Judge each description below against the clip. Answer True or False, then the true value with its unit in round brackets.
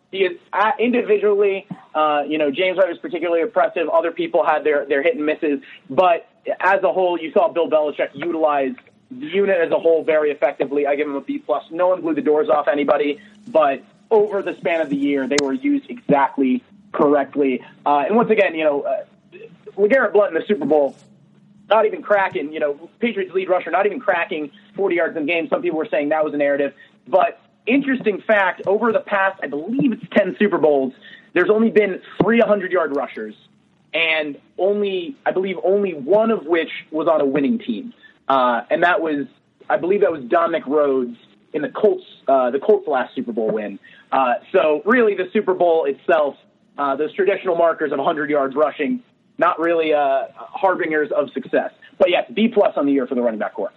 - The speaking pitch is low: False (175 Hz)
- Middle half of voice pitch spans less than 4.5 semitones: False (5.6 semitones)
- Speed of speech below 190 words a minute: False (200 wpm)